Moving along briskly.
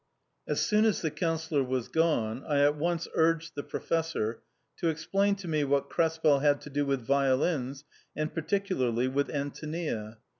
No: average, 160 wpm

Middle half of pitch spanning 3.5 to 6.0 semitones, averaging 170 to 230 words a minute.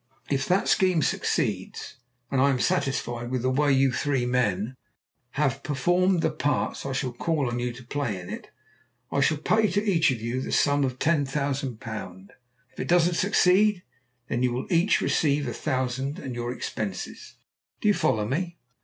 Yes: average, 4.8 semitones; average, 180 wpm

